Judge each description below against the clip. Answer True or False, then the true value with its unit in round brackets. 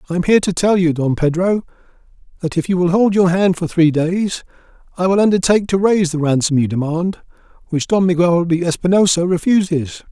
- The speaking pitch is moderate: True (175 Hz)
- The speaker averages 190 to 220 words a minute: True (195 wpm)